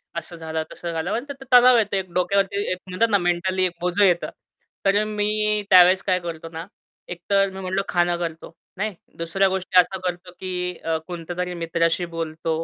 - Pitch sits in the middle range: Yes, medium, 180 Hz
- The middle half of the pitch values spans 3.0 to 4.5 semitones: No, narrow, 2.4 semitones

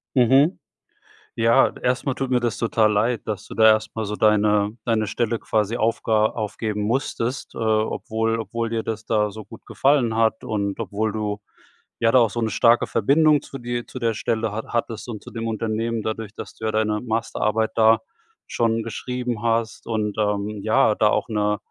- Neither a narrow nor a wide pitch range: No, narrow, 1.5 semitones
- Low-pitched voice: Yes, low, 110 Hz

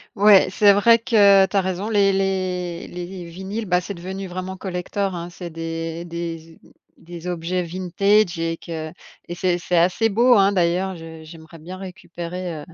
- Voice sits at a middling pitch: Yes, medium, 180 Hz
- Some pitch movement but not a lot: No, narrow, 2.3 semitones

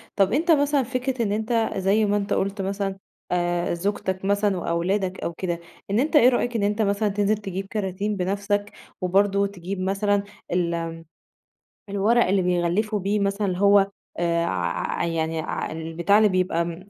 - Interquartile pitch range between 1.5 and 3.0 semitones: Yes, average, 2.7 semitones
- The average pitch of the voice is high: Yes, high, 200 Hz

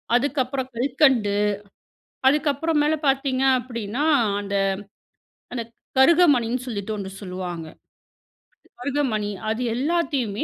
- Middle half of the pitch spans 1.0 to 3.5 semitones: No, average, 5.1 semitones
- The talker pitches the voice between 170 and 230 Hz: No, very high, 255 Hz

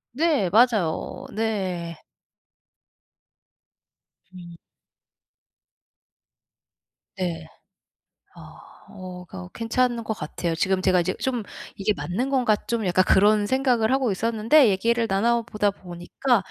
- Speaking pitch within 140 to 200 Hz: No, high, 210 Hz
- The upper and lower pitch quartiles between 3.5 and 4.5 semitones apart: Yes, average, 4.2 semitones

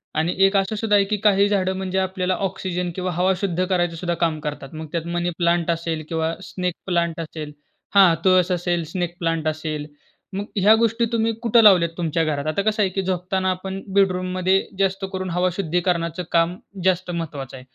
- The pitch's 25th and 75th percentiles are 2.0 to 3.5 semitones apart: Yes, narrow, 2.4 semitones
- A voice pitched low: No, medium, 180 Hz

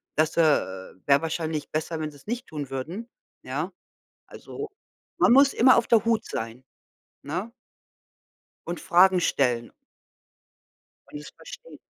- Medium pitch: Yes, medium, 160 Hz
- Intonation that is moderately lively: No, wide, 7.3 semitones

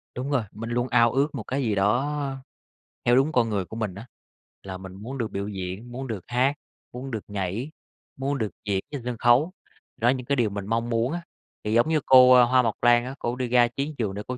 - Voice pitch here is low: Yes, low, 120 Hz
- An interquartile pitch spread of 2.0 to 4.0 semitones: Yes, average, 3.3 semitones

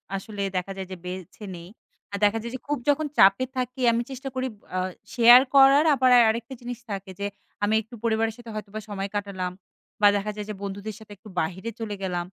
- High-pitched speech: Yes, high, 215 Hz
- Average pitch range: Yes, average, 3.6 semitones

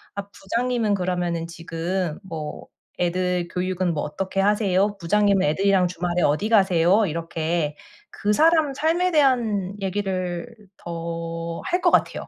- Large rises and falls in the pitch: No, average, 3.5 semitones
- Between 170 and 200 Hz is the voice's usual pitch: Yes, medium, 185 Hz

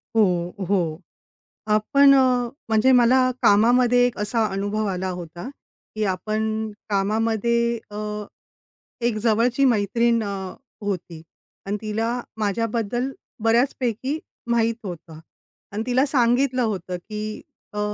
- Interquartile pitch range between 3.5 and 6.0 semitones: No, average, 2.9 semitones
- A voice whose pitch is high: Yes, high, 220 Hz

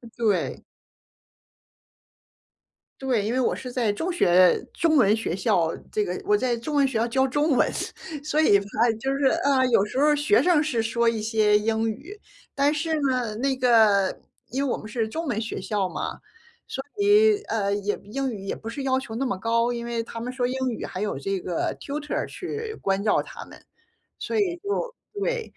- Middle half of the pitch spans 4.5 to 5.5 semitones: Yes, average, 5.1 semitones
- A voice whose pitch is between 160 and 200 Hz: No, high, 240 Hz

